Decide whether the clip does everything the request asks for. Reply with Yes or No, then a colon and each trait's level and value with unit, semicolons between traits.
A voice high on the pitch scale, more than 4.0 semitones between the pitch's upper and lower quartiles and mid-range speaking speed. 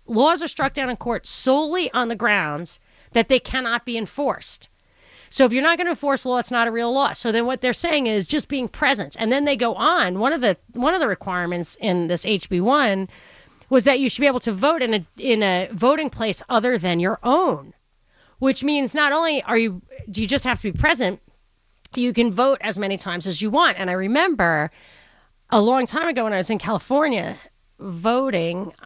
No: high, 240 Hz; average, 4.7 semitones; fast, 220 wpm